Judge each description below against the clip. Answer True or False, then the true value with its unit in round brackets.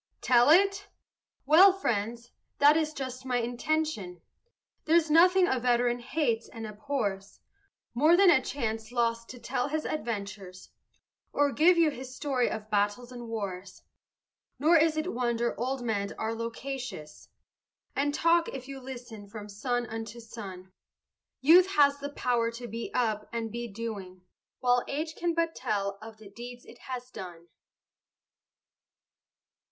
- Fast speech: False (145 wpm)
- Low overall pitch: False (245 Hz)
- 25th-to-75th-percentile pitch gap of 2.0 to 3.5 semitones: False (4.7 semitones)